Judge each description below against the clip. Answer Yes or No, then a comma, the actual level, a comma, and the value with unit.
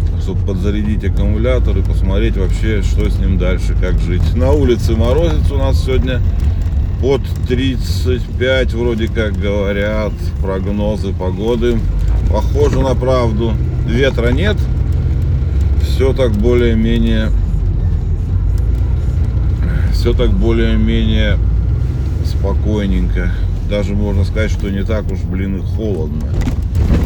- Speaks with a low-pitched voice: Yes, very low, 95 Hz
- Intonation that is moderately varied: Yes, average, 3.6 semitones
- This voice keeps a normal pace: No, slow, 105 wpm